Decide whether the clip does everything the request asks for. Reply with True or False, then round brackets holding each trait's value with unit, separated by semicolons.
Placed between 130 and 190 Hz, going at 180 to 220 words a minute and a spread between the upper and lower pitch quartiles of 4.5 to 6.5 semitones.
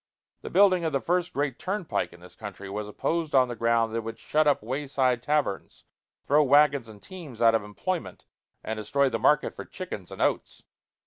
True (135 Hz; 205 wpm; 5.2 semitones)